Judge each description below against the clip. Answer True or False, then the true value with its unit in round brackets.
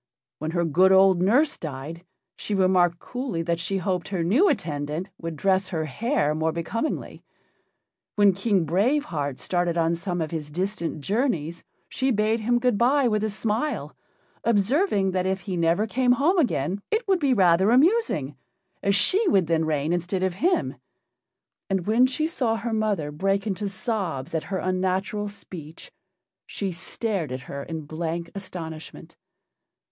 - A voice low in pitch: False (190 Hz)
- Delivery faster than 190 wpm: False (160 wpm)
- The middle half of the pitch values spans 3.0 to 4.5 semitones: False (5.1 semitones)